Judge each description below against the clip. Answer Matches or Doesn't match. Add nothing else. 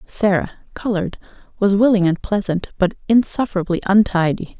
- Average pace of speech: Doesn't match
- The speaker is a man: Doesn't match